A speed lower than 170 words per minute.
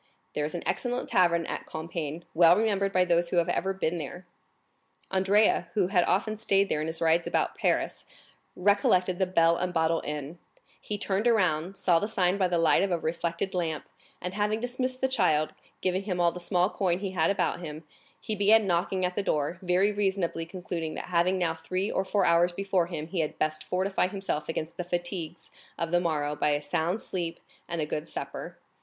No: fast, 205 wpm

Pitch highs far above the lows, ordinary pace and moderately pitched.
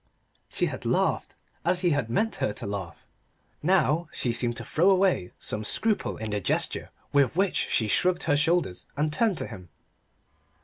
Yes: wide, 8.5 semitones; average, 175 wpm; medium, 150 Hz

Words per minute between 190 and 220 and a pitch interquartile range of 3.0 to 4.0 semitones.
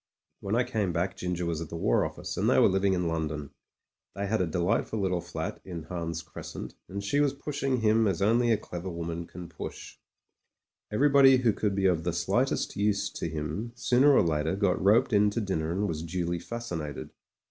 No: fast, 205 wpm; average, 5.0 semitones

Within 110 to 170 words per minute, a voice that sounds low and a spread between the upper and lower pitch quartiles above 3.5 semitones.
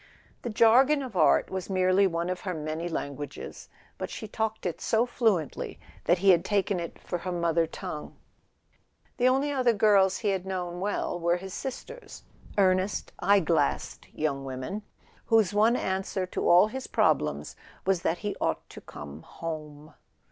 No: average, 165 wpm; medium, 185 Hz; average, 4.0 semitones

